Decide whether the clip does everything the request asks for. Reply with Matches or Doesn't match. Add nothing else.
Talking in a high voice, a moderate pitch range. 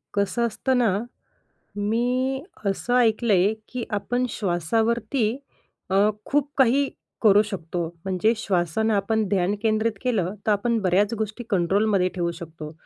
Matches